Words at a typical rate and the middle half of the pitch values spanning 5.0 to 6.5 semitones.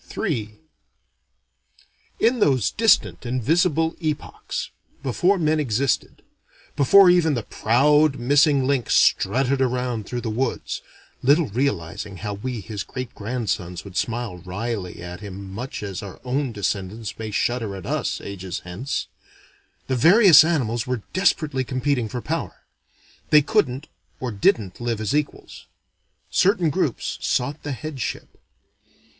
No: slow, 125 wpm; wide, 5.6 semitones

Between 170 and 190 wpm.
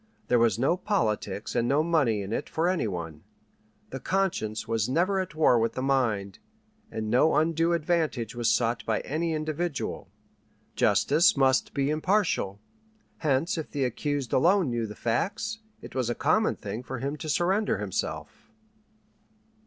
No: average, 160 wpm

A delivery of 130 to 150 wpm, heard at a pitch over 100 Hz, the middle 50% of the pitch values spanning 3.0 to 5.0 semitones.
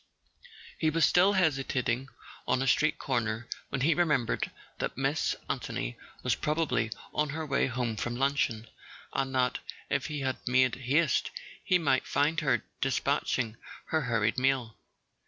Yes: average, 140 wpm; low, 135 Hz; average, 3.9 semitones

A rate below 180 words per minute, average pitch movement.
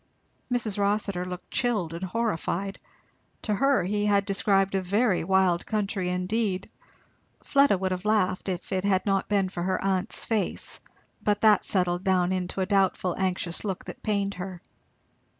No: average, 160 wpm; narrow, 2.1 semitones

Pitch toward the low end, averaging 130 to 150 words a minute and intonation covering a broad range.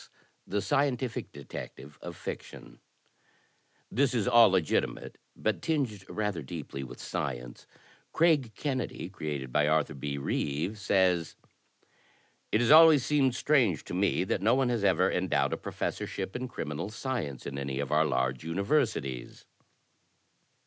Yes: very low, 95 Hz; average, 140 wpm; wide, 9.0 semitones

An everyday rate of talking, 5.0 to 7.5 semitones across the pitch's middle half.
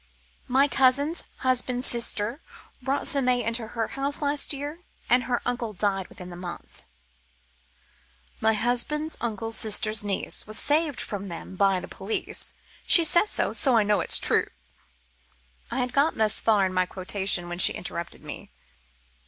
Yes: average, 160 wpm; average, 5.3 semitones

